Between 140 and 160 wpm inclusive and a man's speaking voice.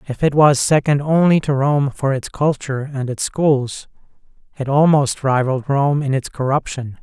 No: average, 170 wpm; male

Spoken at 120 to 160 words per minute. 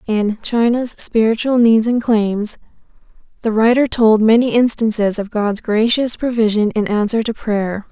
Yes: average, 145 wpm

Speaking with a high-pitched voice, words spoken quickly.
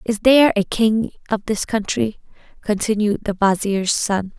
No: high, 210 Hz; average, 150 wpm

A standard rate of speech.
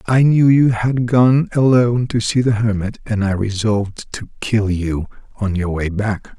Yes: average, 190 wpm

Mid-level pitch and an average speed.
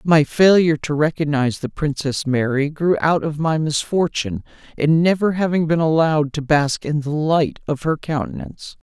Yes: medium, 150 Hz; average, 170 wpm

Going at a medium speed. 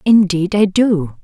Yes: average, 145 wpm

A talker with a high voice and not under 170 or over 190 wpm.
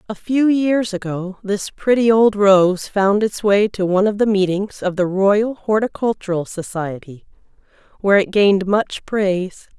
No: high, 200 Hz; average, 160 wpm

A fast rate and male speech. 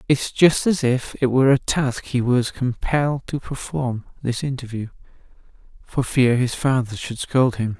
No: average, 155 wpm; male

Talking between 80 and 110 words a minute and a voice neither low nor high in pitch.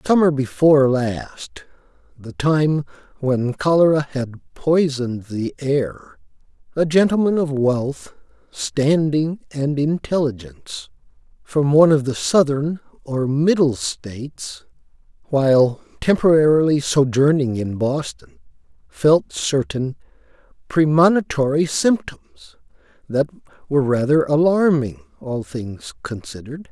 Yes: slow, 95 wpm; medium, 145 Hz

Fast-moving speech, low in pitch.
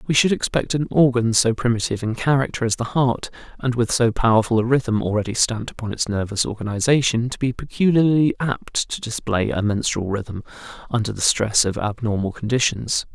No: average, 180 wpm; low, 120 Hz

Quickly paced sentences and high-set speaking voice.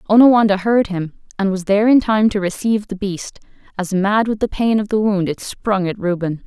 Yes: fast, 225 wpm; high, 200 Hz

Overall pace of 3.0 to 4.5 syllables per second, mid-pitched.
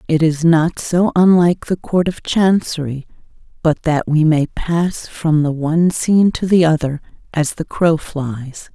Yes: 4.2 syllables/s; medium, 160 Hz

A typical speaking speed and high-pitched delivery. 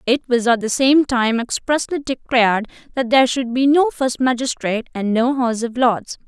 Yes: average, 190 wpm; very high, 250 Hz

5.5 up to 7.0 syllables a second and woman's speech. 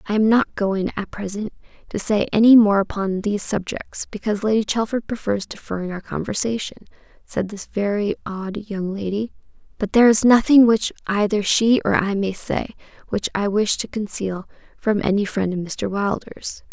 No: 5.0 syllables/s; female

